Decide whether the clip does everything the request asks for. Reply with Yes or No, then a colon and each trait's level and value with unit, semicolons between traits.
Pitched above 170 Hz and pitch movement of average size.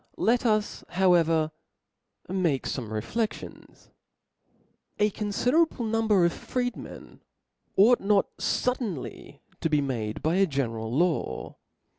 No: medium, 185 Hz; wide, 7.4 semitones